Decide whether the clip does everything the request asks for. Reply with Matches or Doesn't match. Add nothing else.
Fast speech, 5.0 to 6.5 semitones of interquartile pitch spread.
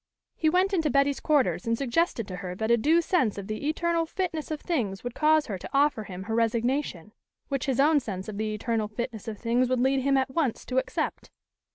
Matches